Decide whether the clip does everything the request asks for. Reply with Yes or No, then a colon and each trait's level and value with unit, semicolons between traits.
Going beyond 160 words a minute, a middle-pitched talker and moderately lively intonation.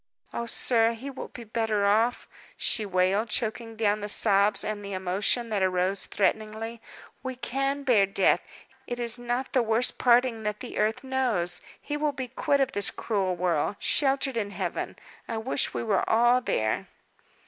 No: average, 170 wpm; high, 225 Hz; average, 3.4 semitones